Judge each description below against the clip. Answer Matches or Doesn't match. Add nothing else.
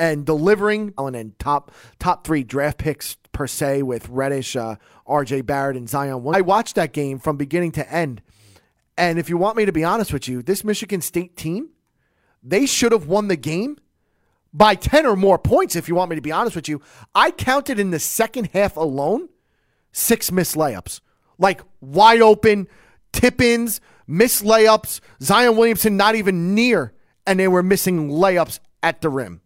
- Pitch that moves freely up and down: Matches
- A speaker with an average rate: Matches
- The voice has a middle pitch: Matches